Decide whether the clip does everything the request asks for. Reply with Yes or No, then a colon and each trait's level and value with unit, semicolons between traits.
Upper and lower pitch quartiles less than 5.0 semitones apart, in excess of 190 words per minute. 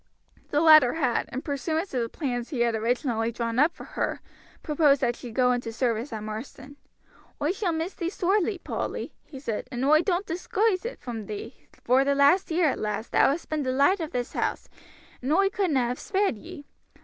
No: wide, 5.6 semitones; fast, 205 wpm